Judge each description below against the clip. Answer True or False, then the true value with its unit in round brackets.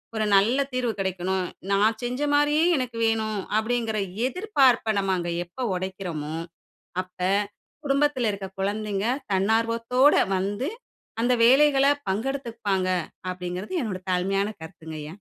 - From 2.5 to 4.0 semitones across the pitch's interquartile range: False (4.8 semitones)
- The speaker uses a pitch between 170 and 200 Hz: False (215 Hz)